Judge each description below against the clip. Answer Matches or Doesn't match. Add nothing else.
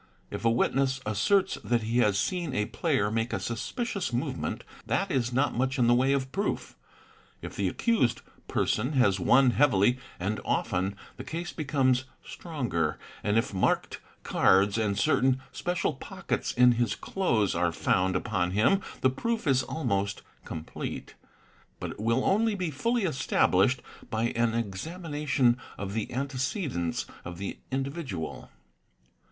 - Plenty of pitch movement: Matches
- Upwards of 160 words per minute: Doesn't match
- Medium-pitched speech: Doesn't match